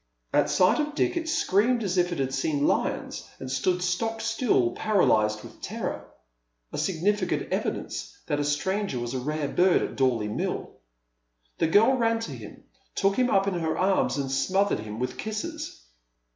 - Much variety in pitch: Yes, wide, 7.7 semitones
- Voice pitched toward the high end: No, medium, 180 Hz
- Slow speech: No, average, 180 wpm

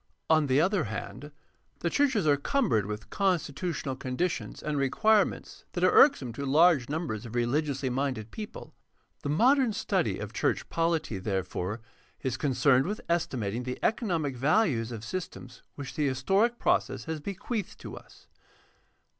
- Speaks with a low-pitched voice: No, medium, 145 Hz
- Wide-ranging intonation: Yes, wide, 6.3 semitones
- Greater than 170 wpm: No, average, 150 wpm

